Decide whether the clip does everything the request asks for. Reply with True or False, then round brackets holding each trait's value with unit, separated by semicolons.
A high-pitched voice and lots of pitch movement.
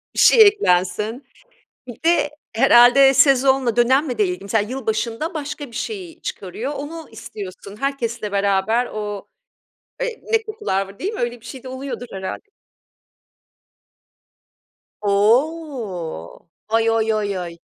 True (240 Hz; 5.7 semitones)